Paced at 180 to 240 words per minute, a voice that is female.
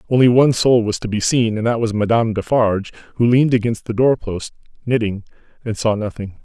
No: average, 195 wpm; male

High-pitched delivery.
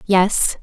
Yes: high, 195 Hz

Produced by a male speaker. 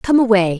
No: female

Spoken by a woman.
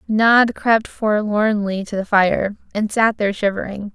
Yes: female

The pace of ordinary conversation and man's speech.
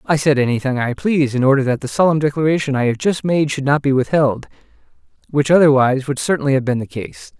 No: fast, 220 wpm; male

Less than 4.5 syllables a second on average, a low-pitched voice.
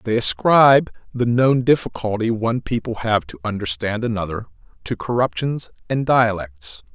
No: 4.9 syllables/s; low, 110 Hz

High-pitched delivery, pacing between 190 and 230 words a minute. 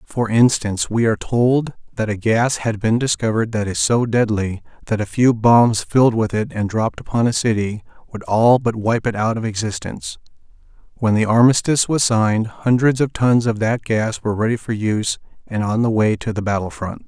No: low, 110 Hz; fast, 205 wpm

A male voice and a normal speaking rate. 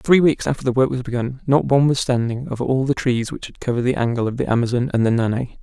No: male; fast, 280 wpm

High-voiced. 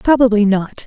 Yes: high, 225 Hz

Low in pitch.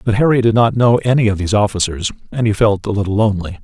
Yes: low, 105 Hz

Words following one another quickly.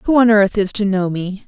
Yes: fast, 285 wpm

